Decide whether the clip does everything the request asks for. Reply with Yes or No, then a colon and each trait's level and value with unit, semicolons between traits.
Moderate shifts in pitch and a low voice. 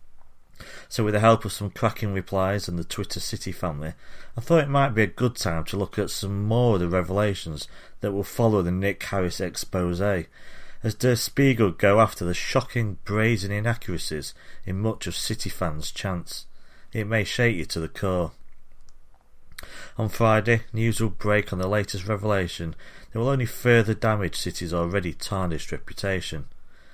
Yes: average, 3.8 semitones; low, 100 Hz